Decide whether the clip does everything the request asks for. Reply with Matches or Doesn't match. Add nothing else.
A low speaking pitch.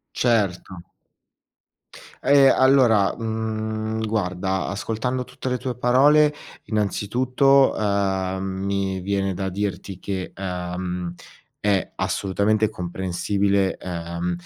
Matches